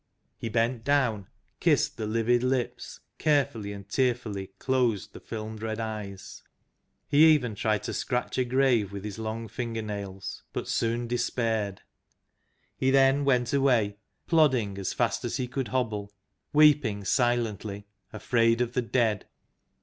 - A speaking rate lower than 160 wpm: Yes, average, 140 wpm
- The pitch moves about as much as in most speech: Yes, average, 3.3 semitones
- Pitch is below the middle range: Yes, low, 115 Hz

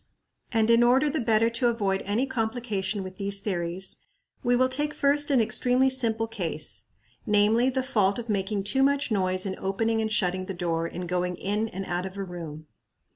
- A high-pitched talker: Yes, high, 210 Hz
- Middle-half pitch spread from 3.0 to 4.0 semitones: No, average, 4.4 semitones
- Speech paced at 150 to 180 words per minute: No, average, 190 wpm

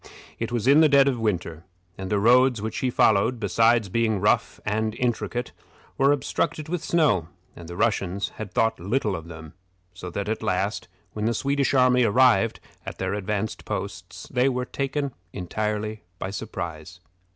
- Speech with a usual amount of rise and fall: Yes, average, 4.4 semitones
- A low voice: Yes, low, 110 Hz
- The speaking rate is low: No, average, 170 wpm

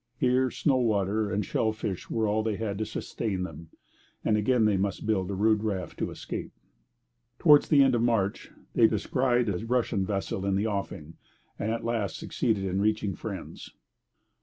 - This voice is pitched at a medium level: No, low, 110 Hz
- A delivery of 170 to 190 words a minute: Yes, average, 180 wpm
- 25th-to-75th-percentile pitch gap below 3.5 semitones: Yes, average, 2.8 semitones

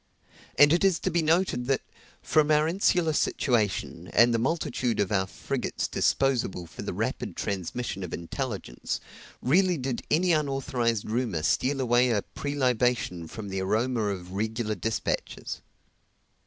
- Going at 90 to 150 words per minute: Yes, average, 145 wpm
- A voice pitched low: Yes, low, 125 Hz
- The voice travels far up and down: Yes, wide, 5.9 semitones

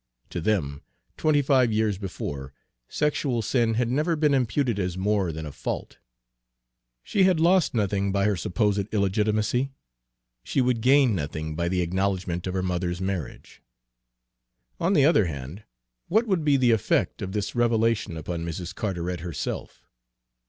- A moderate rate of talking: Yes, average, 150 wpm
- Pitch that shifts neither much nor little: No, wide, 5.9 semitones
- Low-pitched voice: Yes, low, 105 Hz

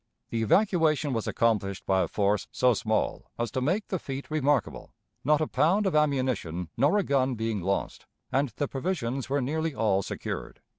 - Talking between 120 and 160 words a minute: No, average, 180 wpm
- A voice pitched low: Yes, low, 130 Hz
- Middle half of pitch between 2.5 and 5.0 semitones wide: No, wide, 5.4 semitones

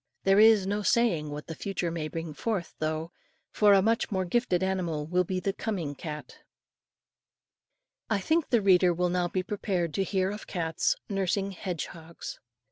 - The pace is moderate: Yes, average, 170 wpm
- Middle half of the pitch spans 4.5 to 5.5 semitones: No, average, 3.1 semitones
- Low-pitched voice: No, medium, 185 Hz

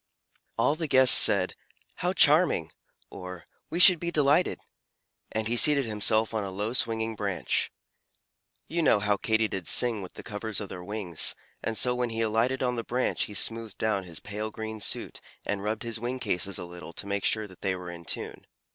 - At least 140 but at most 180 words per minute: No, average, 190 wpm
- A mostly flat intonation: No, average, 3.3 semitones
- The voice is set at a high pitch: No, low, 110 Hz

